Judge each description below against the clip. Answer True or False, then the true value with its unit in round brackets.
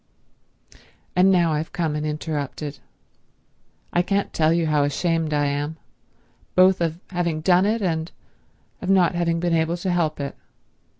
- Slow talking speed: False (145 wpm)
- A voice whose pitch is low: False (165 Hz)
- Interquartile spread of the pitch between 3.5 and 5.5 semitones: False (2.5 semitones)